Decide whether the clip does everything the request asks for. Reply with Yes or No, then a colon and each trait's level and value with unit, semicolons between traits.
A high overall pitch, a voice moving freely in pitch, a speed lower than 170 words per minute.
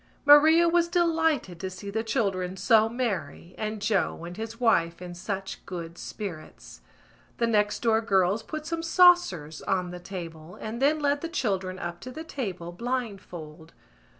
Yes: high, 210 Hz; wide, 6.5 semitones; average, 160 wpm